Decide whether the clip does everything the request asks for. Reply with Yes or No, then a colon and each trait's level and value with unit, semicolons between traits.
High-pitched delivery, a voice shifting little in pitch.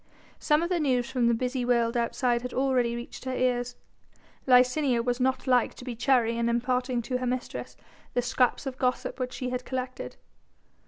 Yes: very high, 250 Hz; narrow, 1.1 semitones